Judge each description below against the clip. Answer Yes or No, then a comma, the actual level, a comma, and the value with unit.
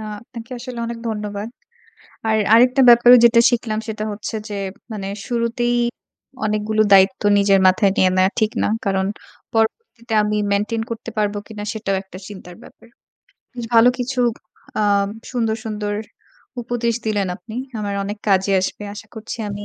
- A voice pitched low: No, high, 215 Hz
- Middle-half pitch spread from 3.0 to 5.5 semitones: No, narrow, 2.4 semitones